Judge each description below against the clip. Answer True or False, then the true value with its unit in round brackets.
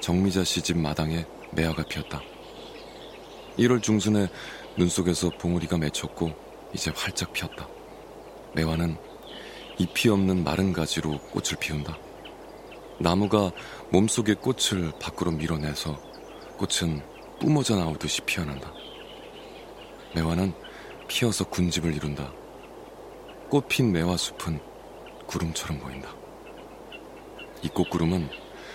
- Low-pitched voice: True (85 Hz)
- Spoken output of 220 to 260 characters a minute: True (230 characters per minute)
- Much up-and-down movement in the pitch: False (3.0 semitones)